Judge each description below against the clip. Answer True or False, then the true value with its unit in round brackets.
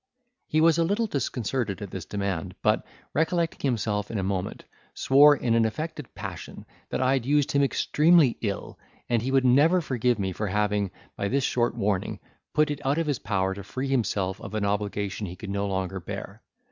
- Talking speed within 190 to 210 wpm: True (195 wpm)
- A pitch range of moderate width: False (5.9 semitones)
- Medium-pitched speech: False (115 Hz)